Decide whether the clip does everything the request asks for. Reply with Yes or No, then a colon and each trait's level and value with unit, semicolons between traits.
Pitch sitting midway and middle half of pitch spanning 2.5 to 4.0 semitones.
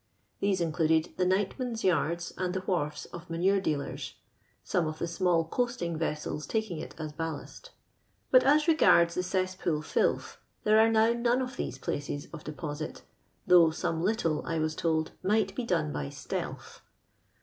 No: medium, 175 Hz; average, 4.6 semitones